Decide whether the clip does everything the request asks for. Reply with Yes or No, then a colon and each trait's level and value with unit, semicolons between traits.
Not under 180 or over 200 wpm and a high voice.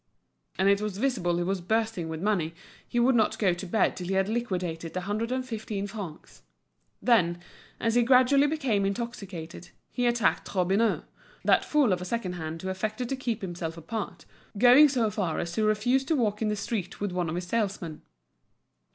Yes: average, 195 wpm; high, 205 Hz